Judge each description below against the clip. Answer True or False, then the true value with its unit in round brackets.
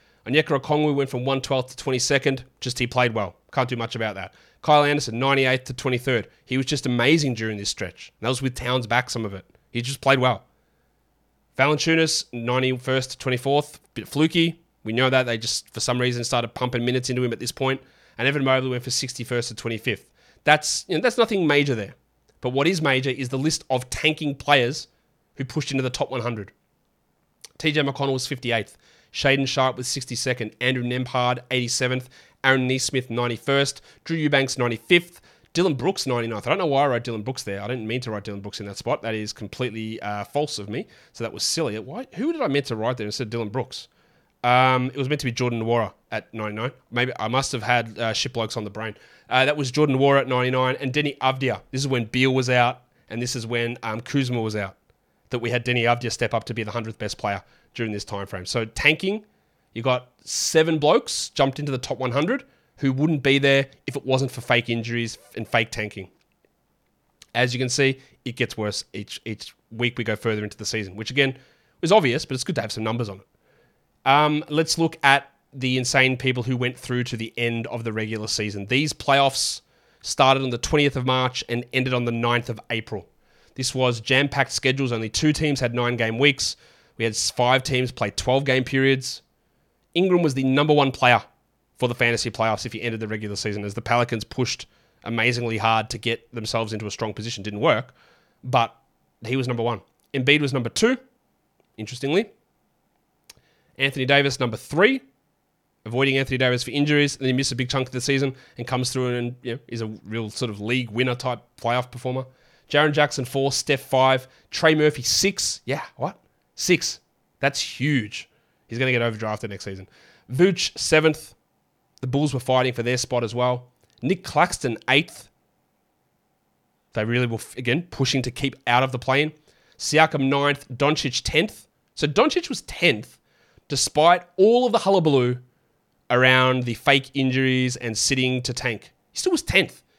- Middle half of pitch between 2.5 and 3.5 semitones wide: True (2.9 semitones)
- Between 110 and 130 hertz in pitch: True (125 Hz)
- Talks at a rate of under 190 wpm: False (200 wpm)